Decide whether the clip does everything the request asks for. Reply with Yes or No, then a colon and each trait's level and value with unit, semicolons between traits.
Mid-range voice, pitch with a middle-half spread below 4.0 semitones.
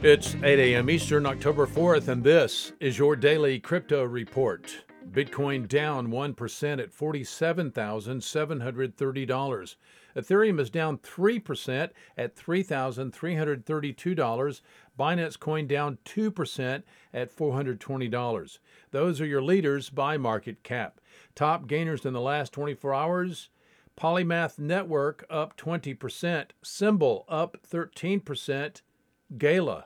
Yes: medium, 145 Hz; average, 3.5 semitones